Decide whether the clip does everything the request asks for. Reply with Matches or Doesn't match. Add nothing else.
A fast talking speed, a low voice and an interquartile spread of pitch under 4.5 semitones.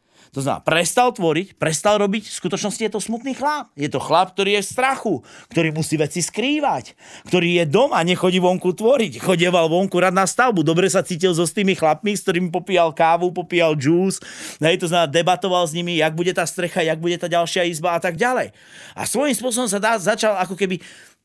Doesn't match